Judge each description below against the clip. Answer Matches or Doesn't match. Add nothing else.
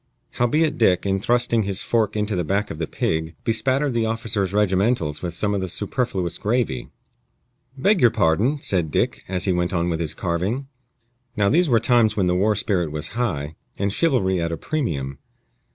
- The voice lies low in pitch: Matches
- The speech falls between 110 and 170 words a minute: Doesn't match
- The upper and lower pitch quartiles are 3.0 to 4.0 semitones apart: Doesn't match